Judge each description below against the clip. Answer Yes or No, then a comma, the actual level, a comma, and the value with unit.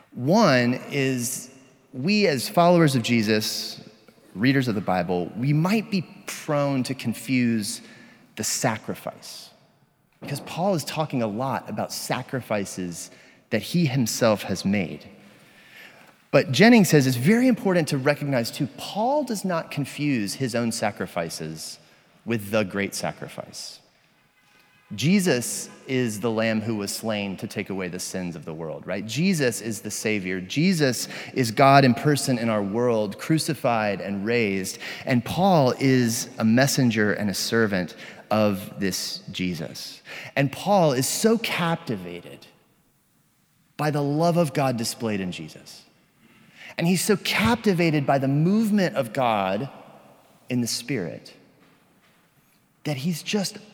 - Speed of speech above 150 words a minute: No, slow, 135 wpm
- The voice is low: Yes, low, 130 Hz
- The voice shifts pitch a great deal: Yes, wide, 6.5 semitones